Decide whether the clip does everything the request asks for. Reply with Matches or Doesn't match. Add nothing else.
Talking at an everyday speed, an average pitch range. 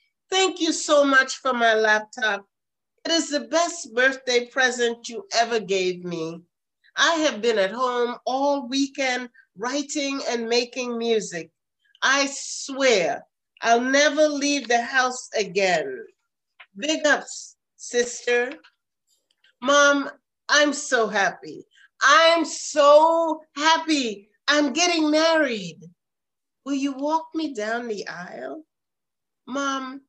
Doesn't match